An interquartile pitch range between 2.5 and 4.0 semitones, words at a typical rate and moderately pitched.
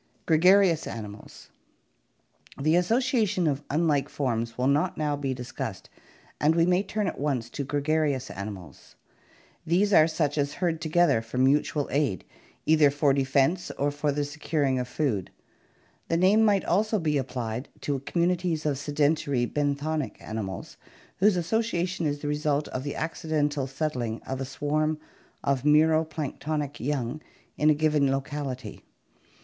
Yes: average, 3.2 semitones; average, 145 wpm; medium, 150 Hz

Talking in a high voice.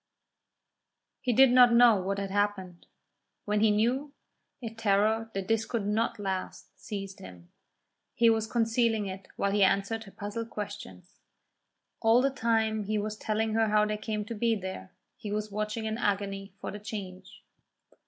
Yes: high, 210 Hz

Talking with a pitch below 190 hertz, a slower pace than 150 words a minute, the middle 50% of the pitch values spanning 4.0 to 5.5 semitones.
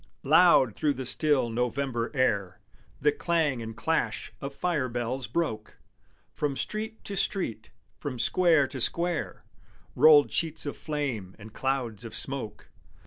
Yes: low, 135 Hz; average, 140 wpm; average, 5.1 semitones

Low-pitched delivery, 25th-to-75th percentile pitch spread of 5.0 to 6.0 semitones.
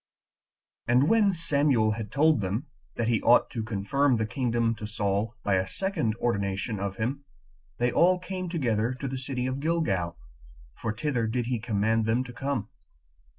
No: low, 120 Hz; average, 4.4 semitones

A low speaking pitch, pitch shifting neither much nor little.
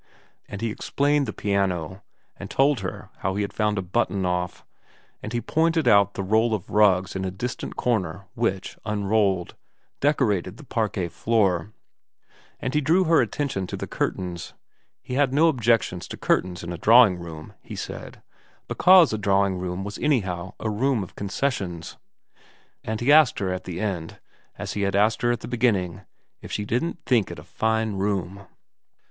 Yes: low, 105 Hz; average, 4.4 semitones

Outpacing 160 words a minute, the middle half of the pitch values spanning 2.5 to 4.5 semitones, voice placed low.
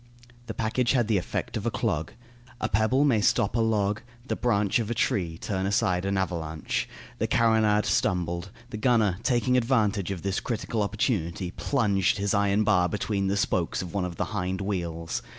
Yes: average, 185 wpm; average, 3.4 semitones; low, 100 Hz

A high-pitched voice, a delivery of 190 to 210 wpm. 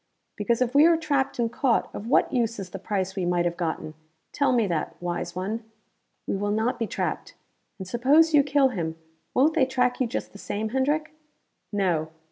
Yes: high, 230 Hz; average, 200 wpm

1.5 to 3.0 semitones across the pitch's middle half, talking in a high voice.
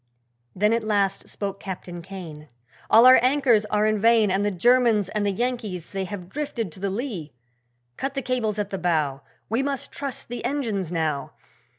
No: average, 4.4 semitones; high, 210 Hz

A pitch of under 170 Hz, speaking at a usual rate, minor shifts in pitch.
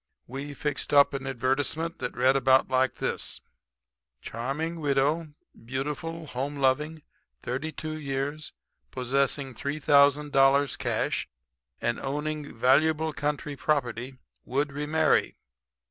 No: medium, 140 Hz; slow, 100 wpm; narrow, 2.1 semitones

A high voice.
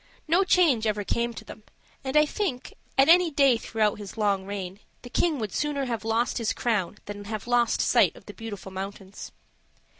Yes: high, 225 Hz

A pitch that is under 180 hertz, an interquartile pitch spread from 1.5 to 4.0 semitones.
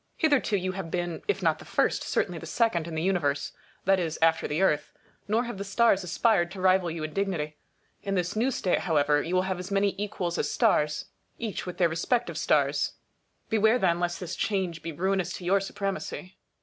No: medium, 185 Hz; average, 2.8 semitones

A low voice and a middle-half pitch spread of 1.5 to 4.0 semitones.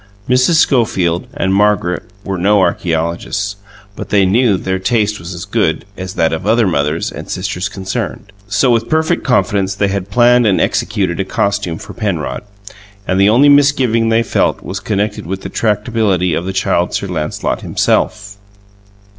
Yes: low, 100 Hz; average, 3.5 semitones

